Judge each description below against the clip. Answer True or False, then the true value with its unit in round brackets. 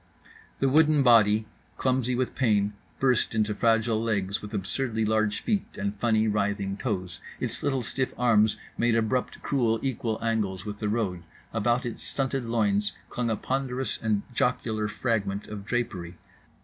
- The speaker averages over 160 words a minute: False (150 wpm)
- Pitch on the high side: False (110 Hz)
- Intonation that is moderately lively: True (3.1 semitones)